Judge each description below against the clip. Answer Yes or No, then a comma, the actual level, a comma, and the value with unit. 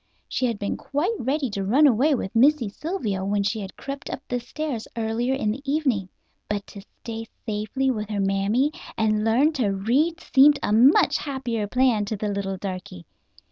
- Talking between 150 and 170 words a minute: No, average, 185 wpm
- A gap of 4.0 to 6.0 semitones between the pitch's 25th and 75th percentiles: Yes, average, 4.9 semitones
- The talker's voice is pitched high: Yes, high, 225 Hz